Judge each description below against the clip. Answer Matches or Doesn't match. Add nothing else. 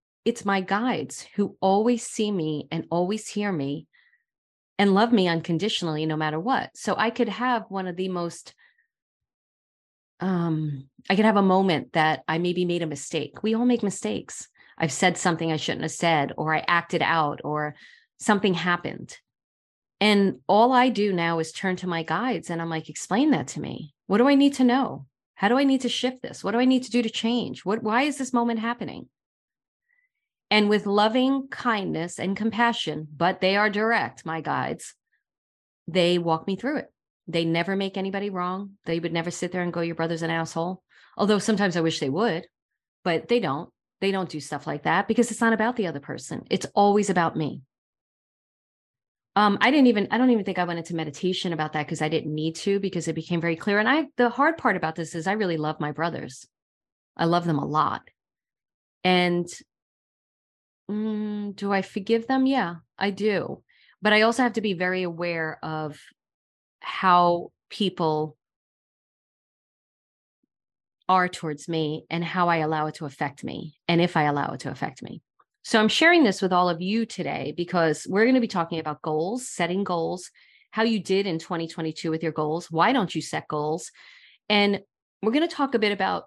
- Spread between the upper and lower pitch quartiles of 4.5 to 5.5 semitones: Matches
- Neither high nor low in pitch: Matches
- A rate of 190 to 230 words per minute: Matches